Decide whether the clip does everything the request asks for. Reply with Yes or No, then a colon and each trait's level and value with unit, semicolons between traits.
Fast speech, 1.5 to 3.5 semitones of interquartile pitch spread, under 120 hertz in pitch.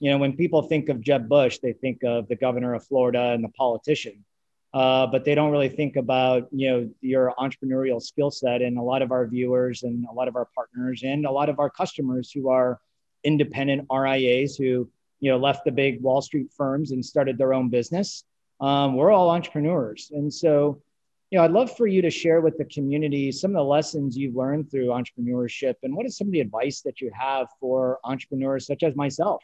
No: fast, 220 wpm; narrow, 2.5 semitones; low, 135 Hz